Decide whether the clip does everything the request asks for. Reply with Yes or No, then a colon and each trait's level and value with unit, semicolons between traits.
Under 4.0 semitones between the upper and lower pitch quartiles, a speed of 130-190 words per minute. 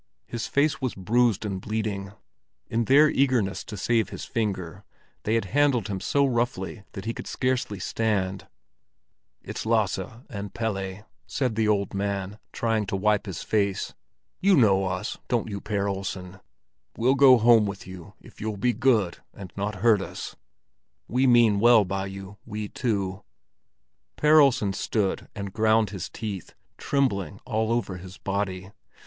Yes: average, 3.3 semitones; average, 155 wpm